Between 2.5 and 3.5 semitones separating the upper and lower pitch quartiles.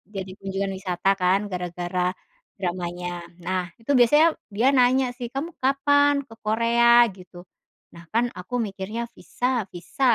No: wide, 5.4 semitones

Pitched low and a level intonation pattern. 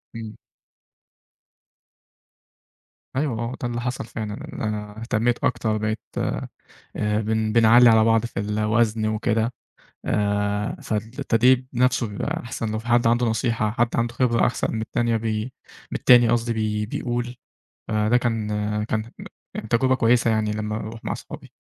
Yes: low, 110 Hz; narrow, 1.9 semitones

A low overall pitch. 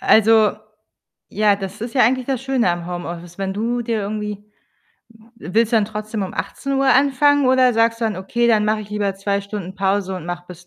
No: high, 215 Hz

